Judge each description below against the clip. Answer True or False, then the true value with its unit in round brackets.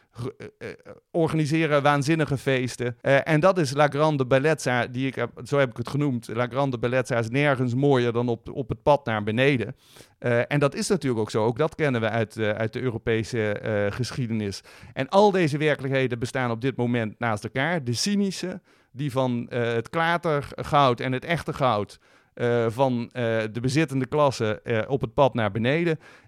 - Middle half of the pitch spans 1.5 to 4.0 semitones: True (3.6 semitones)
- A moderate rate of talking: True (185 wpm)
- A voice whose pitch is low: True (130 Hz)